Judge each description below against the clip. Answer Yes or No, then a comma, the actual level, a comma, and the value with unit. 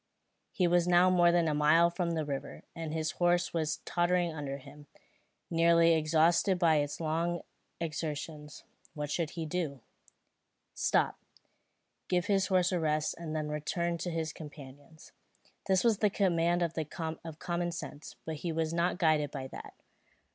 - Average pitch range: No, narrow, 2.2 semitones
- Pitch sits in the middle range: Yes, medium, 165 Hz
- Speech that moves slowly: No, average, 155 wpm